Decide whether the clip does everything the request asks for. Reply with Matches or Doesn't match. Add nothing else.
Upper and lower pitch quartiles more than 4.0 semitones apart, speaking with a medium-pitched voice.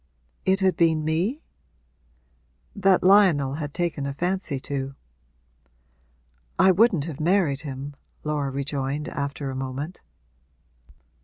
Matches